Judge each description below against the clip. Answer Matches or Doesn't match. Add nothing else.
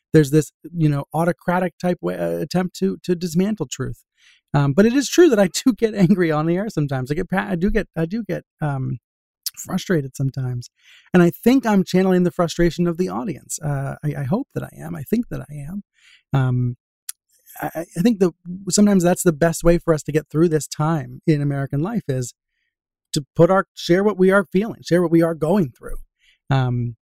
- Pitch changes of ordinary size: Matches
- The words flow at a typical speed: Doesn't match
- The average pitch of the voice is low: Doesn't match